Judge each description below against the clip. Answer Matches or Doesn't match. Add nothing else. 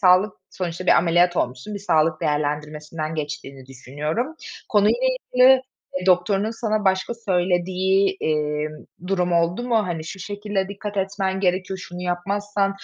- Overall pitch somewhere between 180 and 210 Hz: Matches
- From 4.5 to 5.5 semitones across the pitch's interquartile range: Doesn't match